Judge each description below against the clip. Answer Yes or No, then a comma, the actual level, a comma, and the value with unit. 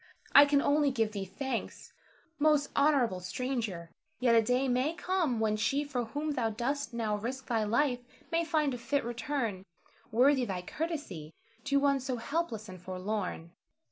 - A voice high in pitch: Yes, very high, 250 Hz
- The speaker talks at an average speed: Yes, average, 165 wpm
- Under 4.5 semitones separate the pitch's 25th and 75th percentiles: No, average, 4.8 semitones